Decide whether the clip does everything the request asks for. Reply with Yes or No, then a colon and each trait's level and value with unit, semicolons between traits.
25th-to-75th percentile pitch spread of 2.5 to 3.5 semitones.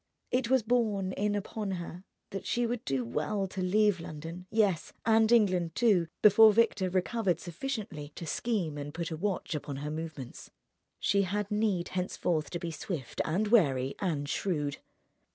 No: average, 5.0 semitones